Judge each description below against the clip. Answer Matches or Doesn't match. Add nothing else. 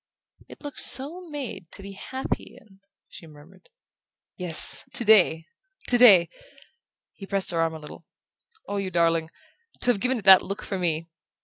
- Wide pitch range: Matches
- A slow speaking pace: Doesn't match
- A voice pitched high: Matches